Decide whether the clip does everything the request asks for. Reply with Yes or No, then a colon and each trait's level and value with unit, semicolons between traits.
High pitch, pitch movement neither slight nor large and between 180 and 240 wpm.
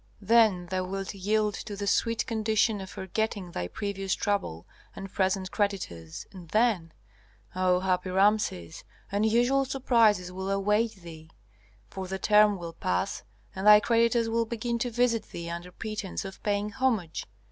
No: high, 200 Hz; average, 3.1 semitones; average, 150 wpm